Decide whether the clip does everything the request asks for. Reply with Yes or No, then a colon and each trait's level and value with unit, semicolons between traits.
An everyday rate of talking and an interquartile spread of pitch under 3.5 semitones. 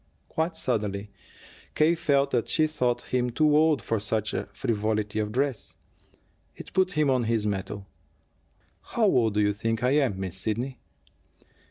No: average, 155 wpm; wide, 5.5 semitones